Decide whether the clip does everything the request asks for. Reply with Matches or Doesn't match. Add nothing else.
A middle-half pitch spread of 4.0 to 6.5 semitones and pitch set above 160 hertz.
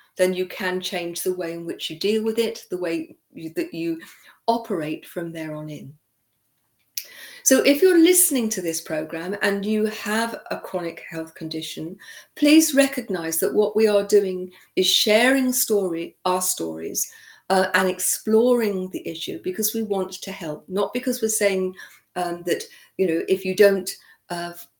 Matches